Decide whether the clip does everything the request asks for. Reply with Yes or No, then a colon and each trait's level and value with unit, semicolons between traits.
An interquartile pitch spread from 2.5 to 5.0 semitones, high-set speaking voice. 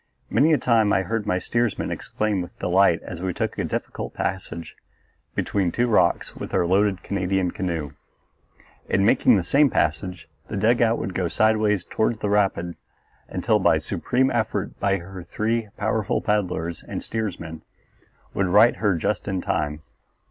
No: average, 3.7 semitones; very low, 95 Hz